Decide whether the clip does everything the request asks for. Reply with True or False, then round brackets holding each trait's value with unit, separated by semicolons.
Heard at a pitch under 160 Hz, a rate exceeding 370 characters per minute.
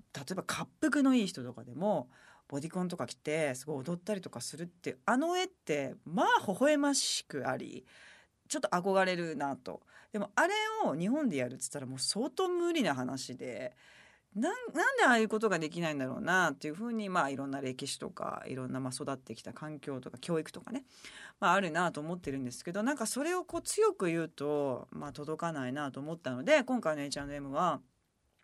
False (170 Hz; 395 characters per minute)